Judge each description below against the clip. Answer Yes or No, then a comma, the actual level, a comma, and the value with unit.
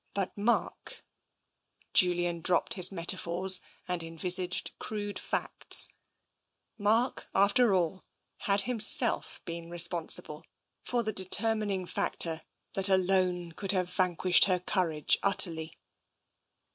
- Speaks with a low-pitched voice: No, medium, 185 Hz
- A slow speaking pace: Yes, slow, 105 wpm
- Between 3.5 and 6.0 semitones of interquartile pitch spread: No, average, 2.7 semitones